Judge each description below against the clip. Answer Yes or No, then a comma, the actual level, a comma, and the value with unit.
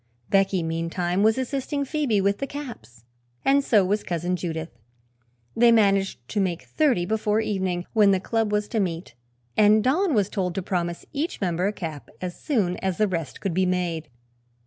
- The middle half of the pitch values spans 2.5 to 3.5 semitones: No, average, 3.9 semitones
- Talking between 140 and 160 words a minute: No, average, 180 wpm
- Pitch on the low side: No, high, 195 Hz